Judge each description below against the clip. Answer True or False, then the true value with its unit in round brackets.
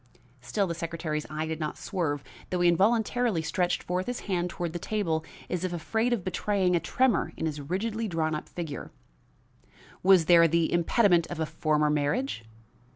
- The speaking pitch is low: False (175 Hz)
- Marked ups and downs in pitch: False (3.5 semitones)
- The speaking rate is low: False (175 wpm)